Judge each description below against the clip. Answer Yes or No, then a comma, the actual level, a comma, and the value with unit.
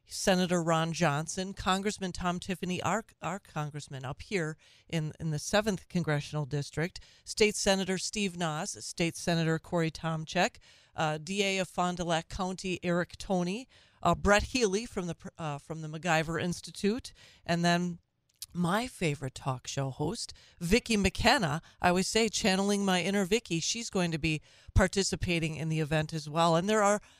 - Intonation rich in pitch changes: No, average, 3.4 semitones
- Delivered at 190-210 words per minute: No, average, 160 wpm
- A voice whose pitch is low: No, medium, 175 Hz